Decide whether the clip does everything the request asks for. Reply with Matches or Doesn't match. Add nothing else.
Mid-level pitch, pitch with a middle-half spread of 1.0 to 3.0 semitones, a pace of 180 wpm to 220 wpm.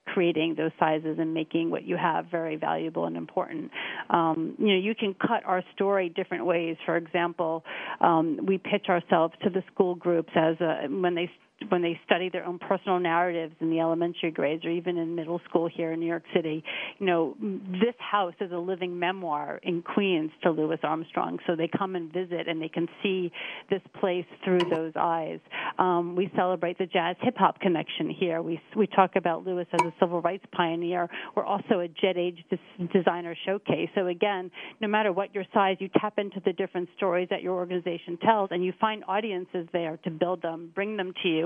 Matches